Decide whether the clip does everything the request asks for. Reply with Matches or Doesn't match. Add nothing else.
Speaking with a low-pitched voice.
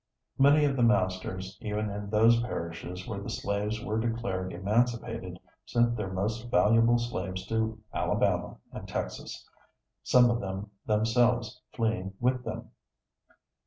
Matches